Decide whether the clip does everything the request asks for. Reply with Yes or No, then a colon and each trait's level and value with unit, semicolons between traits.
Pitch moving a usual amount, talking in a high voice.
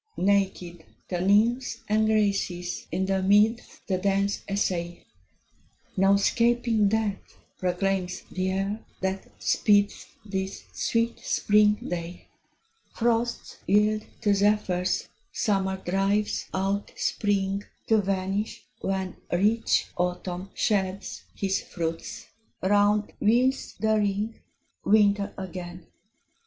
No: narrow, 2.0 semitones; high, 200 Hz